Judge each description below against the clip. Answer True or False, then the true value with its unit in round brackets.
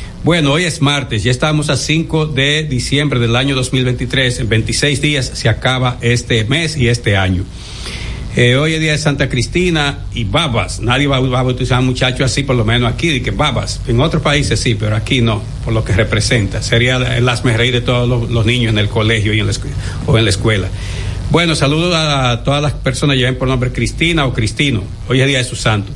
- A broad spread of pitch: False (3.7 semitones)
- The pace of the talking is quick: True (225 wpm)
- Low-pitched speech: True (125 Hz)